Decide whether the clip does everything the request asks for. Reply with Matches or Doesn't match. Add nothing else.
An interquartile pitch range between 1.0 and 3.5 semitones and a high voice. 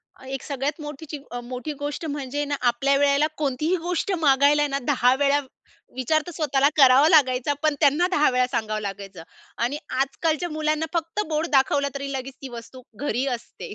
Matches